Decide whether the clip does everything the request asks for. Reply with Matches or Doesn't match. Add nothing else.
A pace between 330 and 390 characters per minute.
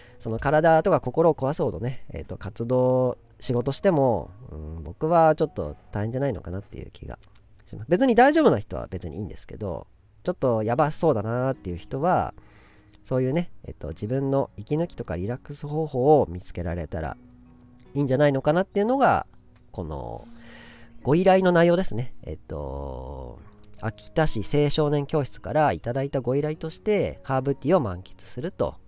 Matches